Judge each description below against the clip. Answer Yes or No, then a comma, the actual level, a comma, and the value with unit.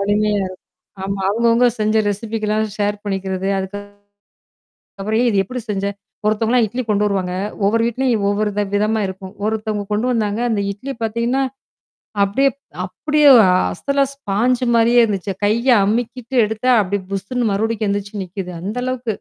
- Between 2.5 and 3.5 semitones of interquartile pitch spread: Yes, average, 2.8 semitones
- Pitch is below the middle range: No, high, 215 Hz